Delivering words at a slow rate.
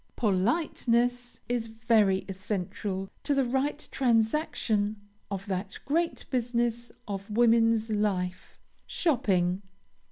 Yes: slow, 95 wpm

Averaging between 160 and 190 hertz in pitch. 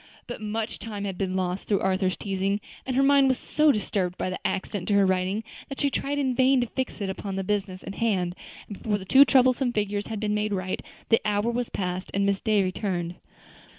No: high, 205 Hz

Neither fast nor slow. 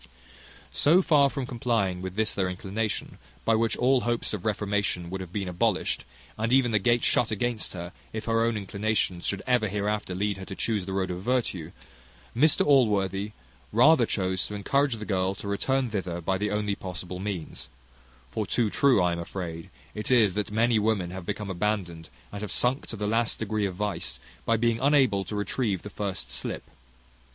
Yes: average, 190 wpm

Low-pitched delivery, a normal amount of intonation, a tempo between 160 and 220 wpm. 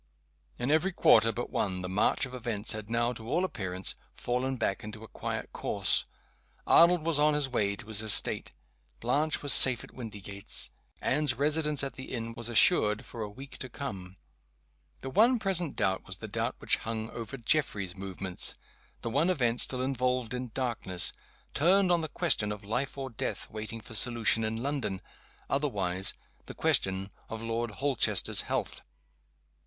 Yes: low, 120 Hz; average, 4.7 semitones; average, 170 wpm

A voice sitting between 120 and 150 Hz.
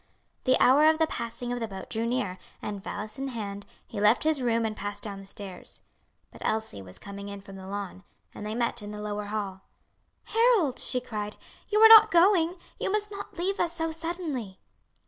No: high, 230 Hz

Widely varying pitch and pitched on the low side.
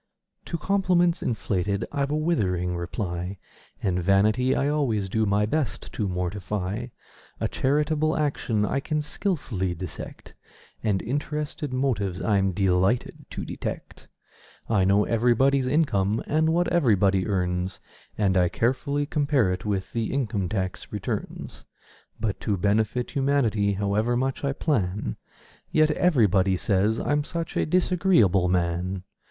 Yes: wide, 6.9 semitones; low, 110 Hz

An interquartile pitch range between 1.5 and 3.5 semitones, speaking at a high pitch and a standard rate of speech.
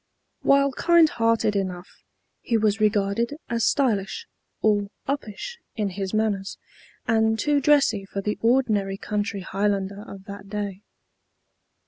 No: average, 2.9 semitones; high, 210 Hz; slow, 125 wpm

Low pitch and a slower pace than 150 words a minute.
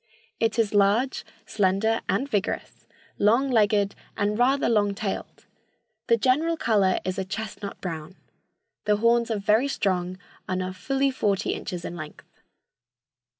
No: high, 210 Hz; average, 140 wpm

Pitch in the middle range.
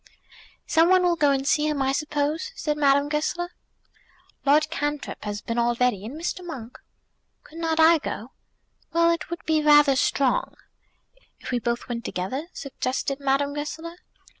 No: very high, 295 Hz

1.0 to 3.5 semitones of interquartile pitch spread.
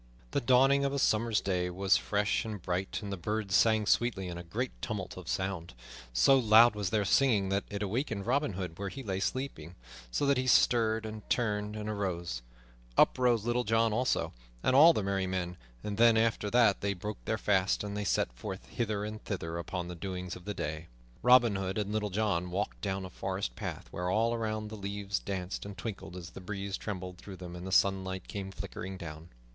Yes: average, 3.0 semitones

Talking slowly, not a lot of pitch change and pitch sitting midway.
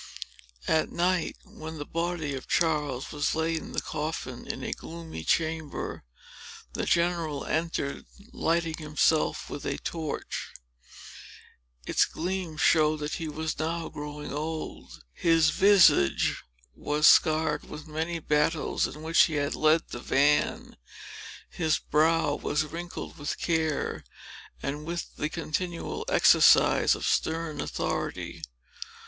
Yes: slow, 130 wpm; narrow, 1.8 semitones; medium, 160 Hz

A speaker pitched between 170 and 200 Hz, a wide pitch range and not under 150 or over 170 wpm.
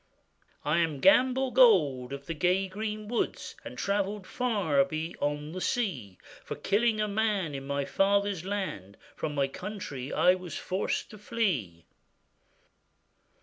No: medium, 185 Hz; wide, 6.6 semitones; average, 140 wpm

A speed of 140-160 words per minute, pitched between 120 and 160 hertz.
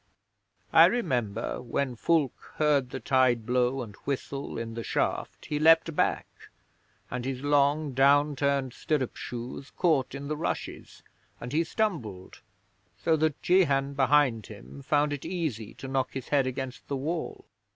Yes: average, 150 wpm; low, 135 Hz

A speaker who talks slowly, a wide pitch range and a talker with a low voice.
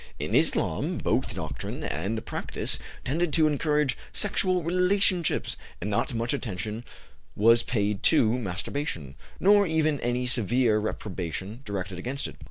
Yes: slow, 130 wpm; wide, 6.9 semitones; low, 120 Hz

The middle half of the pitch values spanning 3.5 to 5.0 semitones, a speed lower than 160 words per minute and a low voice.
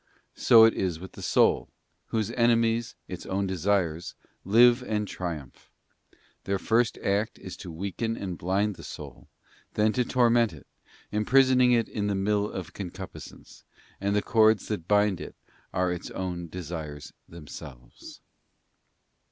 Yes: average, 4.1 semitones; average, 145 wpm; low, 100 Hz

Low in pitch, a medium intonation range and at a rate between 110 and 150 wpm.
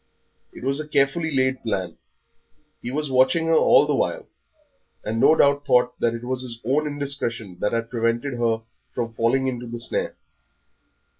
No: low, 125 Hz; average, 3.4 semitones; average, 170 wpm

